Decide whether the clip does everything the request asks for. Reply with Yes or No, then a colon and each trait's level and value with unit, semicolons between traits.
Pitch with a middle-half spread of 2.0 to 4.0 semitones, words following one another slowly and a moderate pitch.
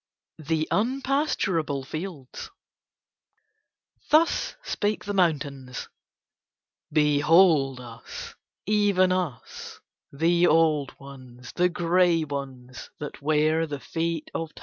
No: average, 4.4 semitones; slow, 95 wpm; medium, 160 Hz